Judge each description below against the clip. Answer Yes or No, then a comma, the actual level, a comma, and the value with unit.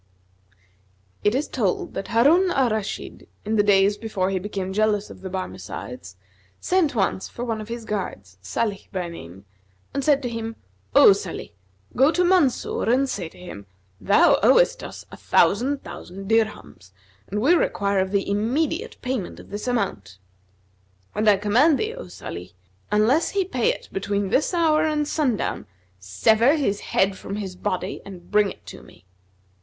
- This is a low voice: No, high, 210 Hz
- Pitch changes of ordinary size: No, wide, 5.7 semitones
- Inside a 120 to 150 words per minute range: No, average, 170 wpm